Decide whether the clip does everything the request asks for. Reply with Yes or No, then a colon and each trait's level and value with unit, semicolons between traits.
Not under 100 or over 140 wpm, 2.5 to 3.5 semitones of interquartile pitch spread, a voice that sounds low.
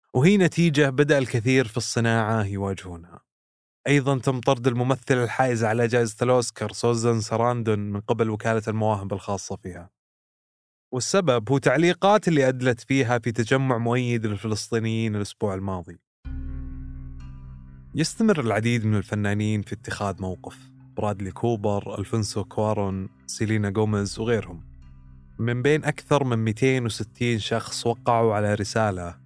No: average, 120 wpm; average, 3.9 semitones; low, 115 Hz